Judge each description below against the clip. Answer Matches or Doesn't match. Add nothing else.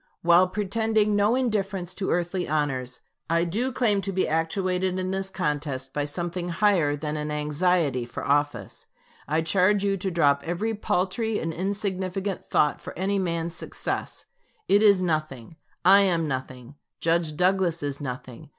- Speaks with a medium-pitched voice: Matches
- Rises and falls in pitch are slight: Doesn't match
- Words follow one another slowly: Doesn't match